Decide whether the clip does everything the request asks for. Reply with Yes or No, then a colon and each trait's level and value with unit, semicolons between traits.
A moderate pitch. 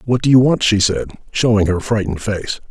No: low, 105 Hz